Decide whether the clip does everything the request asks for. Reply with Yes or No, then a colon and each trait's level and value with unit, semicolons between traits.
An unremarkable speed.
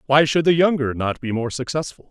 No: fast, 230 wpm